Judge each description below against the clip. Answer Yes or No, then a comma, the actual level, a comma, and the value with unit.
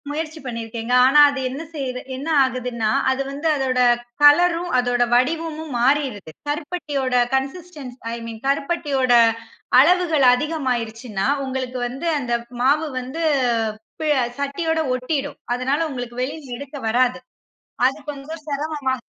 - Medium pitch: No, very high, 270 Hz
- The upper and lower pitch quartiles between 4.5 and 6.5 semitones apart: No, average, 3.4 semitones